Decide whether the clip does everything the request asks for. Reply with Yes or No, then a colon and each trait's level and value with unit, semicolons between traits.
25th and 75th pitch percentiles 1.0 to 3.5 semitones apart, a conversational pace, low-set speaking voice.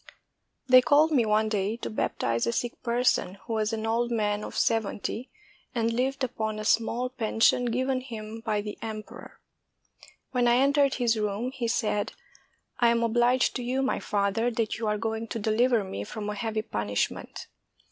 No: narrow, 2.4 semitones; average, 185 wpm; high, 225 Hz